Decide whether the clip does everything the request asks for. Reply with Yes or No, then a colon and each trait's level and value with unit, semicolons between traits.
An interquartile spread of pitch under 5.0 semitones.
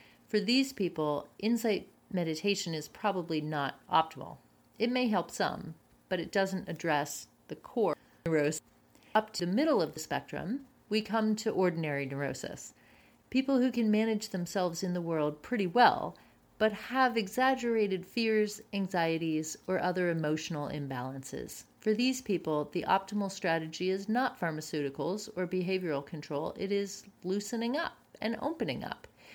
No: wide, 5.5 semitones